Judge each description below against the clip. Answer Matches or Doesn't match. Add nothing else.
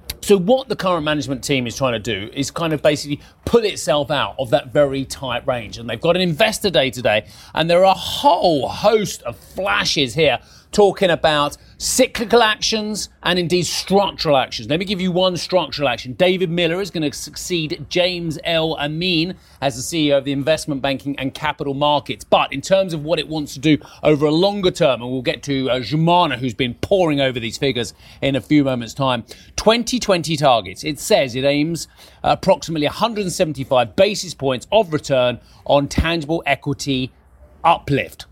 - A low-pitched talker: Doesn't match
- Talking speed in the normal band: Matches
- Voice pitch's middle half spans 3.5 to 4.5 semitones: Doesn't match